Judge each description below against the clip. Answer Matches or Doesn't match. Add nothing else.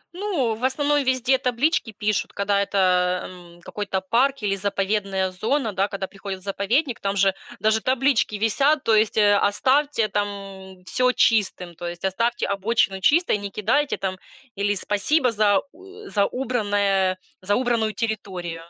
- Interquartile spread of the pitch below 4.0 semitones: Doesn't match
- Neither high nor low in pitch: Doesn't match